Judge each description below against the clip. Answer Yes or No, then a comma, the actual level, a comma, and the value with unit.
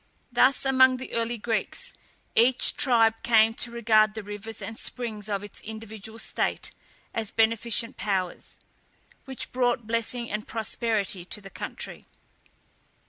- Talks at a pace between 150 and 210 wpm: No, slow, 135 wpm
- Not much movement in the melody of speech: Yes, narrow, 1.9 semitones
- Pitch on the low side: No, high, 225 Hz